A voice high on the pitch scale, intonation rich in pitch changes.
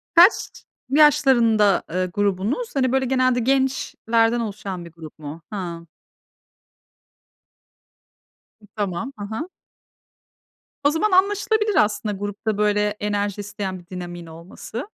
Yes: high, 210 Hz; wide, 5.9 semitones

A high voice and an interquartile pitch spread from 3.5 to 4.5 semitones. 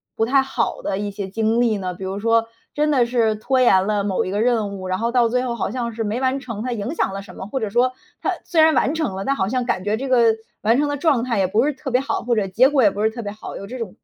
Yes: high, 230 Hz; average, 3.9 semitones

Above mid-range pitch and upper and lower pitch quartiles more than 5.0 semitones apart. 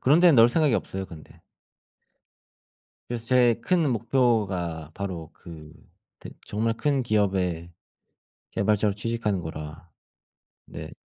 No: low, 105 Hz; wide, 5.6 semitones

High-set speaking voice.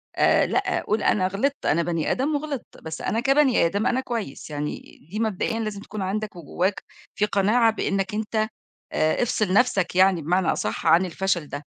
Yes: high, 200 Hz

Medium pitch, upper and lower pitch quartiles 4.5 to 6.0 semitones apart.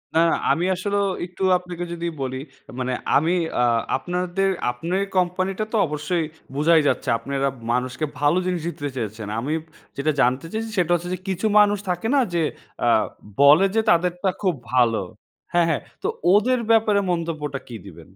Yes: medium, 170 Hz; average, 4.8 semitones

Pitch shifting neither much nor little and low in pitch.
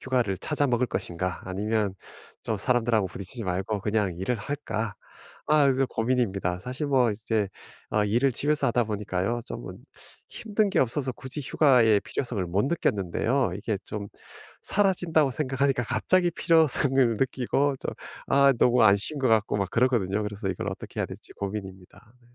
Yes: average, 4.9 semitones; low, 115 Hz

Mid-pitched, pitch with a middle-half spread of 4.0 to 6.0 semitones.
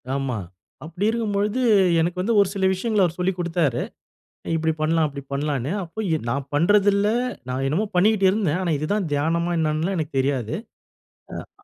Yes: medium, 170 Hz; average, 5.2 semitones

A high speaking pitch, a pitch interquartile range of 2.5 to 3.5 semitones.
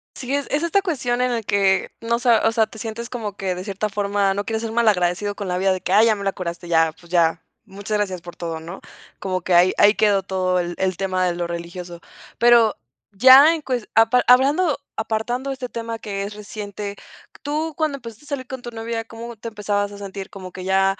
No: high, 210 Hz; average, 3.9 semitones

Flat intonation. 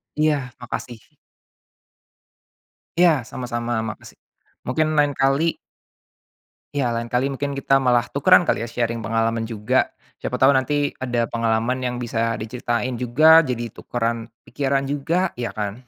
No: average, 3.0 semitones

